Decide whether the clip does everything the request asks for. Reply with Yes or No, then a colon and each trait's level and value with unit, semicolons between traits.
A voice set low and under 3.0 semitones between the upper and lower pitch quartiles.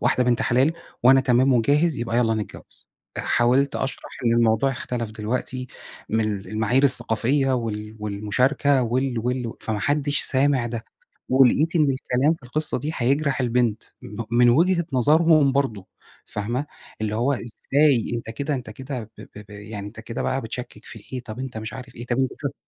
No: low, 125 Hz; average, 3.3 semitones